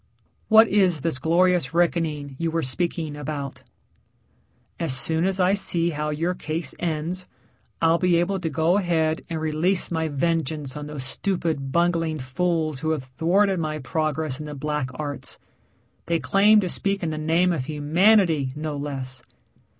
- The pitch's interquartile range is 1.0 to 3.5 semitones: Yes, average, 2.8 semitones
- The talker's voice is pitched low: No, medium, 160 Hz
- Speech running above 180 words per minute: No, average, 160 wpm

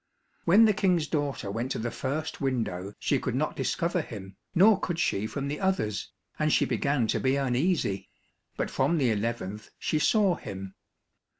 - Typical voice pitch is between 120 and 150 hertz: Yes, low, 135 Hz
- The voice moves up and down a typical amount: No, wide, 7.8 semitones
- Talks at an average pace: Yes, average, 175 wpm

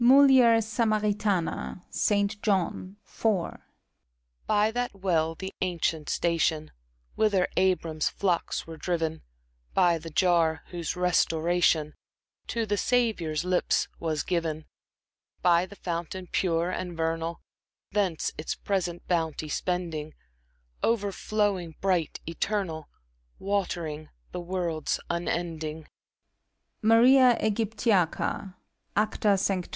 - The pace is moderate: No, slow, 105 wpm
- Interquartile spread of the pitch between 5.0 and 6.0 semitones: No, average, 3.8 semitones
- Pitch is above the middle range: No, medium, 180 Hz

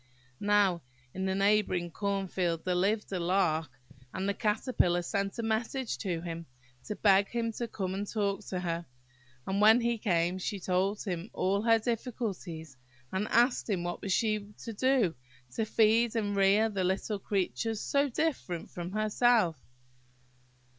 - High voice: Yes, high, 200 Hz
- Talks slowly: No, average, 160 wpm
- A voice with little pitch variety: No, average, 3.5 semitones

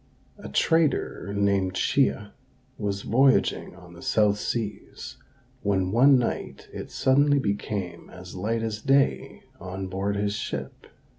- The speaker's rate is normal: No, slow, 130 wpm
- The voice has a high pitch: No, low, 100 Hz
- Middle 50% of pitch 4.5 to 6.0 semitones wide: No, average, 3.7 semitones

